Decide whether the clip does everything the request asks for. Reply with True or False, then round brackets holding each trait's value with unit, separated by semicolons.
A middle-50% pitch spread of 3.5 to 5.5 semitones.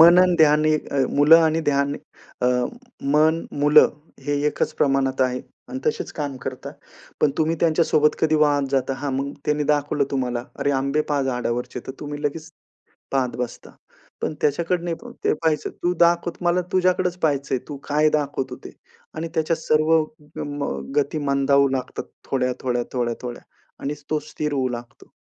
False (2.8 semitones)